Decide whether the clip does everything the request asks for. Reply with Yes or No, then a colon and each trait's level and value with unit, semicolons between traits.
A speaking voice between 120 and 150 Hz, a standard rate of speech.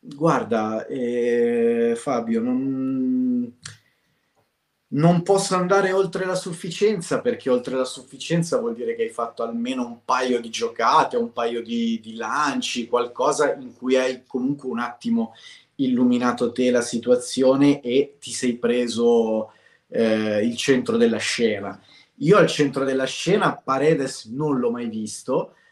Yes: medium, 140 Hz; average, 140 wpm